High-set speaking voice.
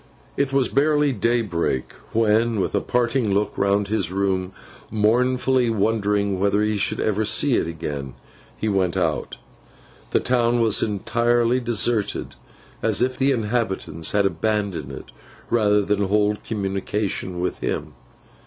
No: low, 105 Hz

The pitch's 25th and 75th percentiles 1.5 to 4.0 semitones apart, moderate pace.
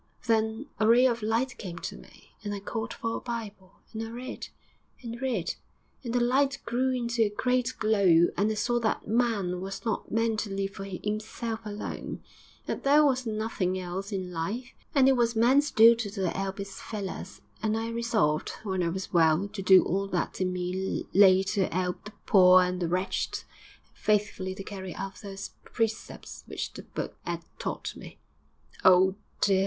Yes: average, 3.6 semitones; average, 185 wpm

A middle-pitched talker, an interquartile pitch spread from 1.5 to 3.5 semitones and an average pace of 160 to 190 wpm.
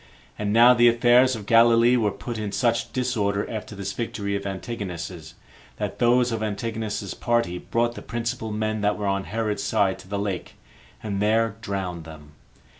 No: low, 110 Hz; average, 2.9 semitones; average, 175 wpm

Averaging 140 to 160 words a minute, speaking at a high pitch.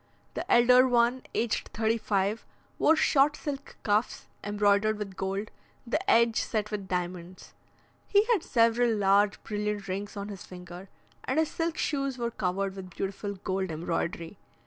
Yes: average, 150 wpm; high, 210 Hz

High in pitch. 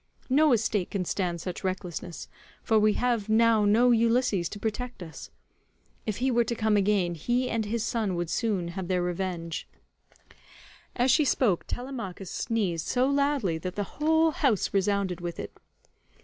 Yes: high, 210 Hz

